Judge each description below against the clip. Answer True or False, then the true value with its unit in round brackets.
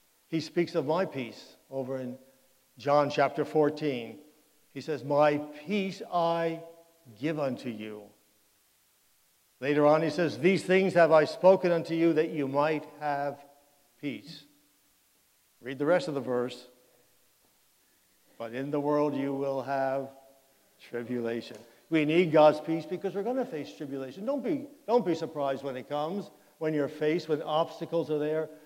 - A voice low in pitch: False (150 Hz)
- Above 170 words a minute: False (155 wpm)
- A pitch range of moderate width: True (3.3 semitones)